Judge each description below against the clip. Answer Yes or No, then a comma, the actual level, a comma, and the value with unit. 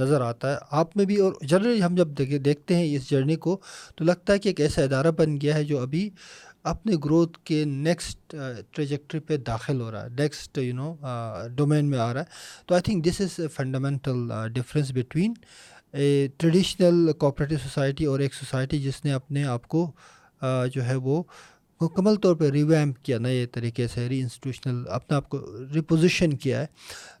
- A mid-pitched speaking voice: Yes, medium, 145 Hz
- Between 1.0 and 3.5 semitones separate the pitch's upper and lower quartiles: No, average, 3.9 semitones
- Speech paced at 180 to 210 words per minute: Yes, fast, 190 wpm